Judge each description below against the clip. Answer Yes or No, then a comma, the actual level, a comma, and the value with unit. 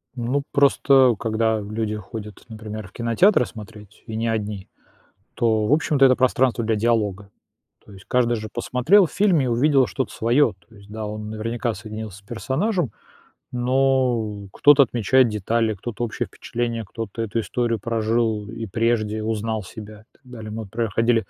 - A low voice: Yes, low, 115 Hz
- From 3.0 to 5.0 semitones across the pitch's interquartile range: No, narrow, 2.4 semitones